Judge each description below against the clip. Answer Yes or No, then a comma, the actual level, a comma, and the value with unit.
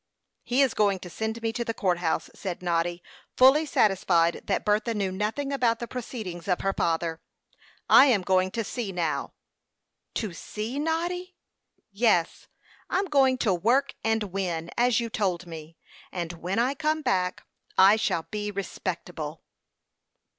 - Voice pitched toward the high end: Yes, high, 205 Hz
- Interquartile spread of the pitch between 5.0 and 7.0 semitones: Yes, wide, 5.4 semitones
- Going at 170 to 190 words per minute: No, average, 155 wpm